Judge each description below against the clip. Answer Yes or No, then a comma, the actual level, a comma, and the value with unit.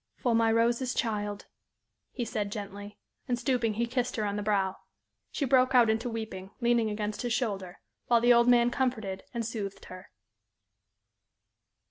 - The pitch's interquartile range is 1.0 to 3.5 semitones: Yes, average, 2.8 semitones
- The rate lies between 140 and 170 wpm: Yes, average, 160 wpm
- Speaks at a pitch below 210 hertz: No, high, 225 Hz